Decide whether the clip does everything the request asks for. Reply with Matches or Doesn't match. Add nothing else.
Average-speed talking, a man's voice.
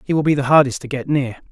Doesn't match